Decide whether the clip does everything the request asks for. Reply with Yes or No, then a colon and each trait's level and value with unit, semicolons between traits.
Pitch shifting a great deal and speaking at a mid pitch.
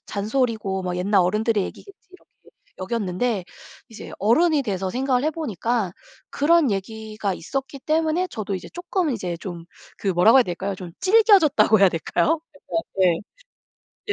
No: wide, 7.3 semitones; high, 220 Hz